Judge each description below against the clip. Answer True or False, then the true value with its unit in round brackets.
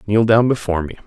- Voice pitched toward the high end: False (105 Hz)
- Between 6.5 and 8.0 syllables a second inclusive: True (7.0 syllables/s)